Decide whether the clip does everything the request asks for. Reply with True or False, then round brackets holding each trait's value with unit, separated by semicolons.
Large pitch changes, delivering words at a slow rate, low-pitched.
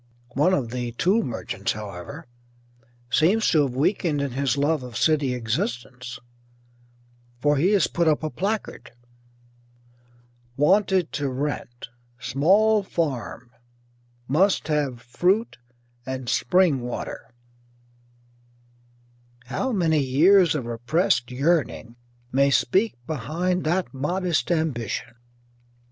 False (6.0 semitones; 105 wpm; 145 Hz)